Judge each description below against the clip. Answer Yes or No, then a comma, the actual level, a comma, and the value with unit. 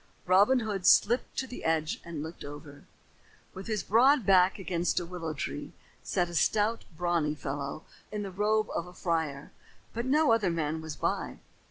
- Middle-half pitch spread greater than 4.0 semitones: Yes, average, 5.1 semitones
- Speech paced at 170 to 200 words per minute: Yes, average, 175 wpm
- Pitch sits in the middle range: Yes, medium, 180 Hz